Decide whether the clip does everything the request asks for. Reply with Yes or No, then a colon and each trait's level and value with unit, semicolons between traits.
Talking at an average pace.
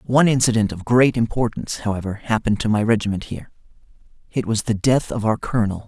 Yes: average, 185 wpm